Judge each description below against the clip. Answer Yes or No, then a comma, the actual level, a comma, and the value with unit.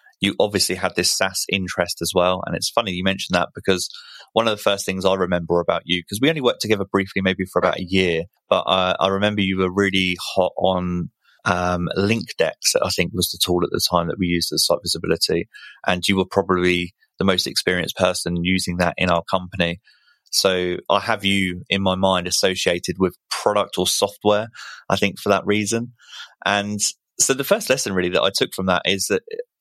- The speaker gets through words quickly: Yes, fast, 210 wpm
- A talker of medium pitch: No, very low, 95 Hz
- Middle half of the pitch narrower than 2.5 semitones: Yes, narrow, 1.8 semitones